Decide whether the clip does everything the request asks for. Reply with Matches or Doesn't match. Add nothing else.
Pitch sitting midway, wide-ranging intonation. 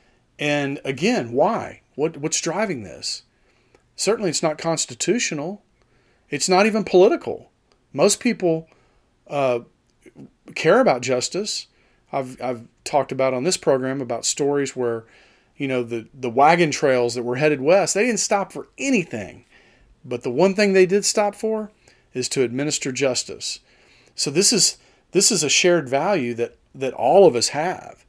Matches